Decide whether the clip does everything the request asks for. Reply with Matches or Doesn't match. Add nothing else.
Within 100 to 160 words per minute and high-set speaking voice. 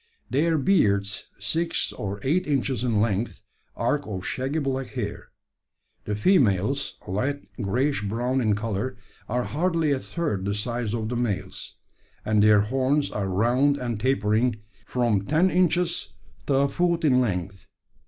Doesn't match